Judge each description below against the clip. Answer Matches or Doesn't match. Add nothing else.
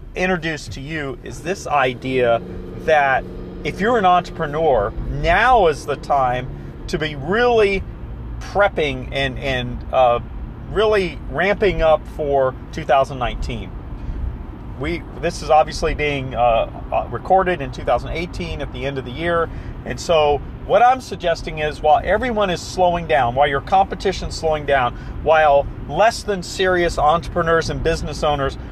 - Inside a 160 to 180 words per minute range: Doesn't match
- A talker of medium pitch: Matches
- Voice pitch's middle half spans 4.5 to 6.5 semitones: Matches